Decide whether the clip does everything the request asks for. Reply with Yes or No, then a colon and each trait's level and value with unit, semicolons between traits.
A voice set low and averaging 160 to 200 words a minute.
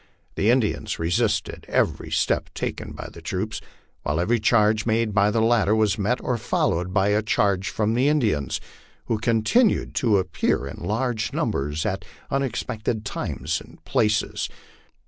No: low, 110 Hz; average, 150 wpm